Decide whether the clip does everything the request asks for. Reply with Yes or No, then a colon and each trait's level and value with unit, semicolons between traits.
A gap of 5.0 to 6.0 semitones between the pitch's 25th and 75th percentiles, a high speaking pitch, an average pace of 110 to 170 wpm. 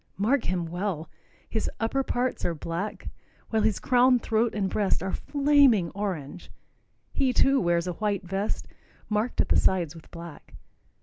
Yes: wide, 5.5 semitones; high, 205 Hz; average, 160 wpm